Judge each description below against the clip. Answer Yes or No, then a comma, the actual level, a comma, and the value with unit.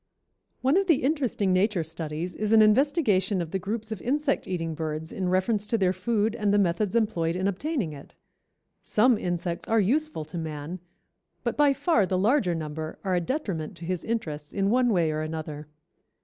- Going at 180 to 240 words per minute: Yes, average, 190 wpm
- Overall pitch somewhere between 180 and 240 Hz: Yes, high, 190 Hz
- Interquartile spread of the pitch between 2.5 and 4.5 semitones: No, wide, 5.4 semitones